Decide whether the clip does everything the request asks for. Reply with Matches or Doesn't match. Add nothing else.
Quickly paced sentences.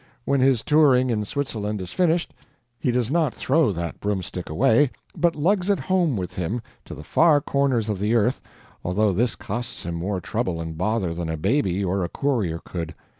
Doesn't match